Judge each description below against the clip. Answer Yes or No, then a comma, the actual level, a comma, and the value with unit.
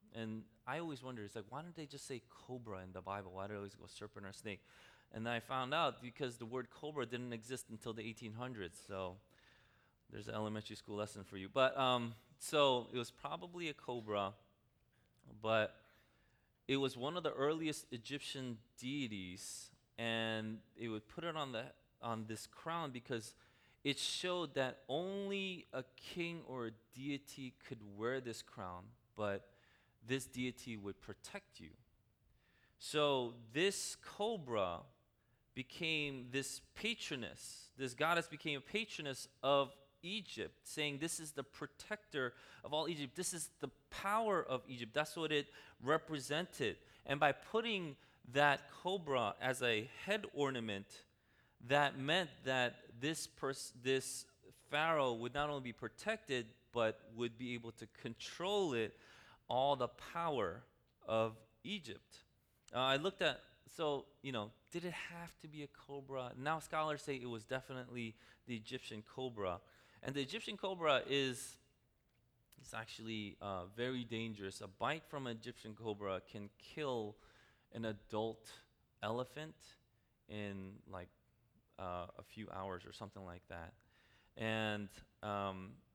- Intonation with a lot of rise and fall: No, average, 4.6 semitones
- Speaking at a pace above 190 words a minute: No, average, 150 wpm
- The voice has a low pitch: Yes, low, 125 Hz